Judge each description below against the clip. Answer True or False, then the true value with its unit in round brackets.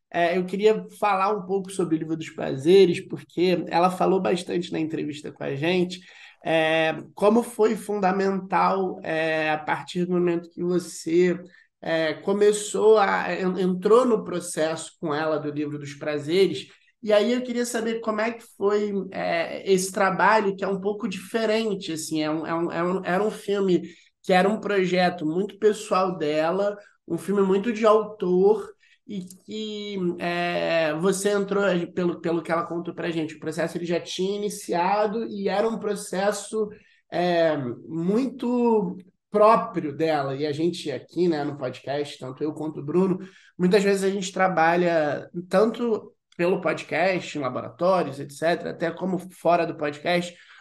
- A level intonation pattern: False (3.7 semitones)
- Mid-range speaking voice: True (180 Hz)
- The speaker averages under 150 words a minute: False (160 wpm)